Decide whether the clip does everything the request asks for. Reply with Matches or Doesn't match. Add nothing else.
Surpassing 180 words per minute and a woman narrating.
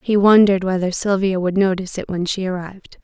Matches